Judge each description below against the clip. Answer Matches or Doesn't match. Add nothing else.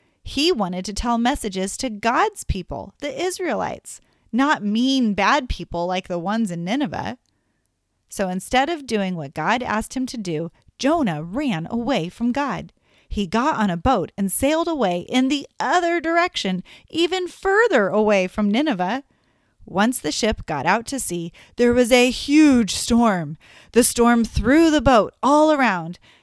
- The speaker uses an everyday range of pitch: Doesn't match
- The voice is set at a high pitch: Matches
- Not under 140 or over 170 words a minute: Matches